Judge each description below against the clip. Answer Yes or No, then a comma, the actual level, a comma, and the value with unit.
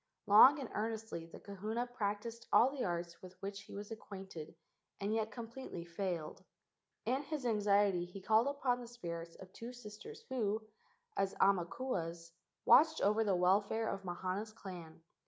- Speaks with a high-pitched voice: Yes, high, 205 Hz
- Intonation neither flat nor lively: Yes, average, 4.1 semitones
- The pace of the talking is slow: No, average, 155 wpm